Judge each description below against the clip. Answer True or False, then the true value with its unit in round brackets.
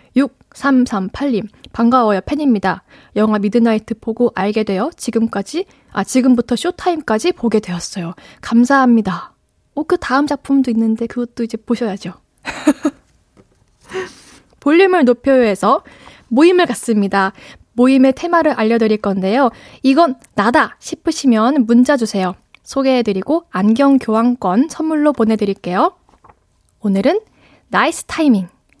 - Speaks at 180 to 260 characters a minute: False (285 characters per minute)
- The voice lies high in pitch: True (245 Hz)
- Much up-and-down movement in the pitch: False (4.8 semitones)